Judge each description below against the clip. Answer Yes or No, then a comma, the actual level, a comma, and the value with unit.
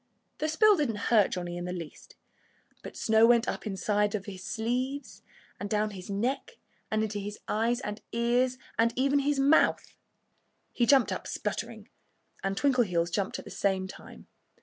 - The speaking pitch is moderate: No, high, 220 Hz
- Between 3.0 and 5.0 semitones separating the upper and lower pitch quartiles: Yes, average, 4.3 semitones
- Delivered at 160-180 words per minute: Yes, average, 170 wpm